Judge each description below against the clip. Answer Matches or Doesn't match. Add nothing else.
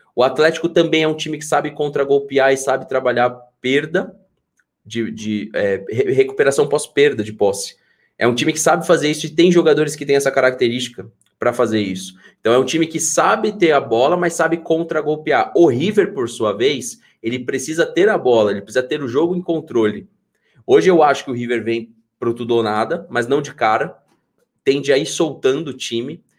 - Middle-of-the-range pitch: Matches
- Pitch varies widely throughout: Matches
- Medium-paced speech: Doesn't match